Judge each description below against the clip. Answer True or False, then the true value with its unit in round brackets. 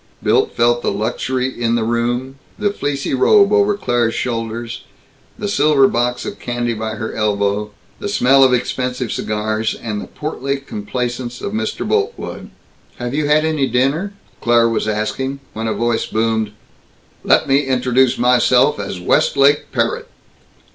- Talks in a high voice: False (125 Hz)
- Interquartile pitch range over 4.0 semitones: False (3.4 semitones)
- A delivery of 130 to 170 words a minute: True (150 wpm)